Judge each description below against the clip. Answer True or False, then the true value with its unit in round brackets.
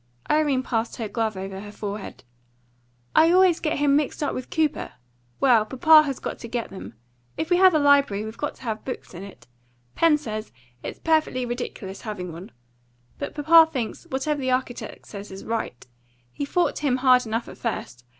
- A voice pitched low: False (255 Hz)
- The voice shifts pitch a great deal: True (5.7 semitones)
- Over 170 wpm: True (190 wpm)